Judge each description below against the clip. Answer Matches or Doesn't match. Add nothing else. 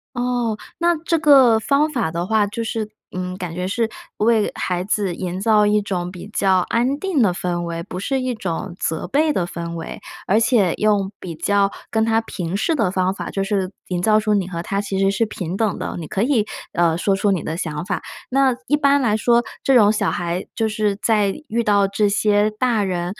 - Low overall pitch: Doesn't match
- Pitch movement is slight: Doesn't match